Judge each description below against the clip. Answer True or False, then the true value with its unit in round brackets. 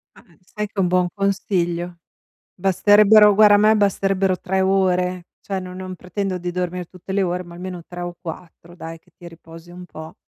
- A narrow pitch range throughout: True (1.8 semitones)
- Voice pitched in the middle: True (180 Hz)